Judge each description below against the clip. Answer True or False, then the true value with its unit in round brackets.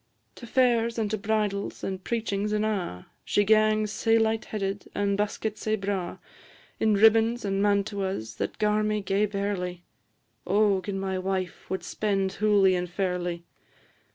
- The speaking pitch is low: False (205 Hz)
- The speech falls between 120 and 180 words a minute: True (155 wpm)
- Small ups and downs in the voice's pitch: True (2.0 semitones)